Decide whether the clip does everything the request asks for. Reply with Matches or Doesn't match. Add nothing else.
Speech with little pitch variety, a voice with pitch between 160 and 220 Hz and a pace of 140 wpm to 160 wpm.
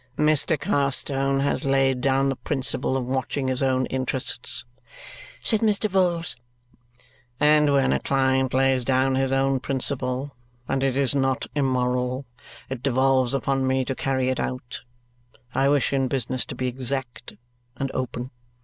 Doesn't match